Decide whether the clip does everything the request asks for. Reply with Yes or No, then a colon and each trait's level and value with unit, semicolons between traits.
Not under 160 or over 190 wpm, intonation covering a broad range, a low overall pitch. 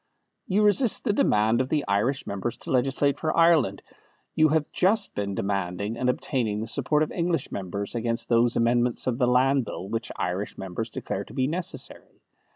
Yes: average, 180 wpm; wide, 6.0 semitones; low, 125 Hz